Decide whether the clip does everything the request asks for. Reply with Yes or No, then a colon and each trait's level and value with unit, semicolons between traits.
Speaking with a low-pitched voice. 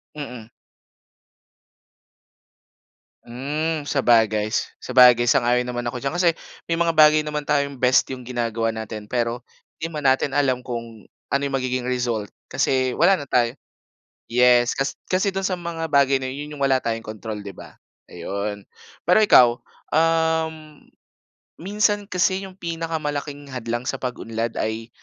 Yes: low, 130 Hz